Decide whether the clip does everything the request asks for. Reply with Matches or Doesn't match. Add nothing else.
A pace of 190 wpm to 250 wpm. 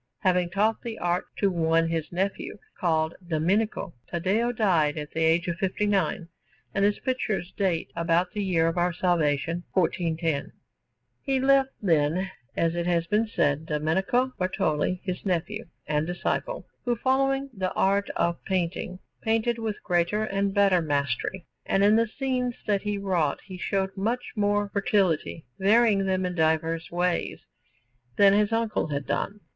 Doesn't match